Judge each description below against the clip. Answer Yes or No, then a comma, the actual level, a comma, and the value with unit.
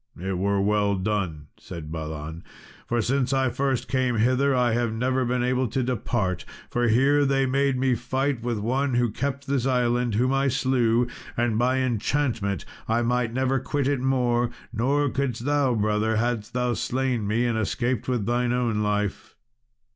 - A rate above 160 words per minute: Yes, average, 170 wpm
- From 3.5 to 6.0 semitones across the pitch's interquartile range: No, average, 3.0 semitones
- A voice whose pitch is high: No, low, 120 Hz